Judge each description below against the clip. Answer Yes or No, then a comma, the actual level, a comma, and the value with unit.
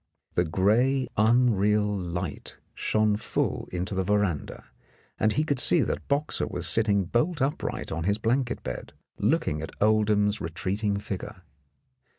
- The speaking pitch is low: Yes, low, 105 Hz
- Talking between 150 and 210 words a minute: No, average, 140 wpm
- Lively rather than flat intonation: No, average, 4.1 semitones